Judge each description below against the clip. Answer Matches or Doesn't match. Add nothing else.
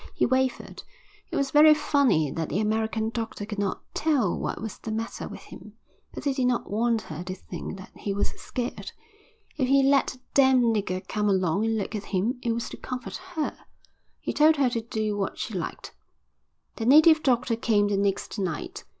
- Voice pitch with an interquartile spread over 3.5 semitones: Matches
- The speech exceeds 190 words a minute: Matches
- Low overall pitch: Doesn't match